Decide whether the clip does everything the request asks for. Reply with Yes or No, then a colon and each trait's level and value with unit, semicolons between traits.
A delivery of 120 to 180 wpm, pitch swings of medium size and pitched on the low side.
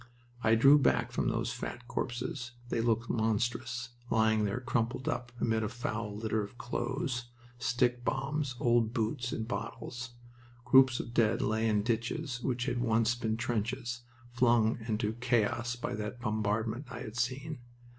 No: average, 150 wpm; narrow, 1.7 semitones; low, 120 Hz